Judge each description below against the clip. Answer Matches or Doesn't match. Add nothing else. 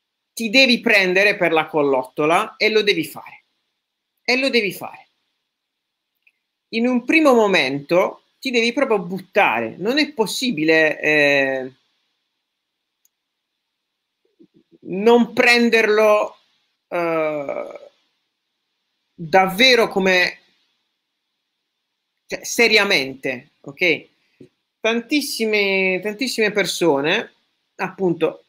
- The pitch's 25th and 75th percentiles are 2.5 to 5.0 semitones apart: Doesn't match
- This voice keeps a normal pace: Doesn't match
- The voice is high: Matches